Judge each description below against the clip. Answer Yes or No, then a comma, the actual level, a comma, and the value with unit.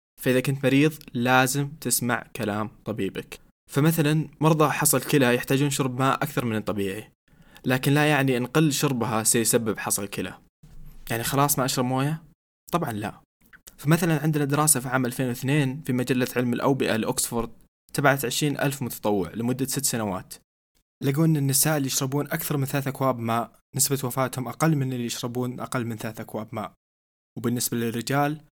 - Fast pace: Yes, fast, 155 wpm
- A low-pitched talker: Yes, low, 130 Hz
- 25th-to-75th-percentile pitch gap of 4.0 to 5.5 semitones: No, average, 3.6 semitones